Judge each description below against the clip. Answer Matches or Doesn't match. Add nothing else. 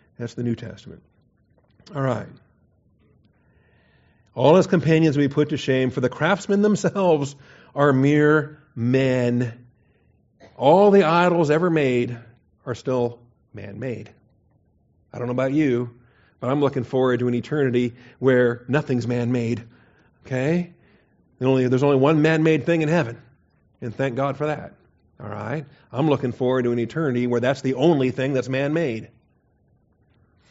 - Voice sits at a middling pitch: Doesn't match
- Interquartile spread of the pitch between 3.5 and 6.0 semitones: Matches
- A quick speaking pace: Doesn't match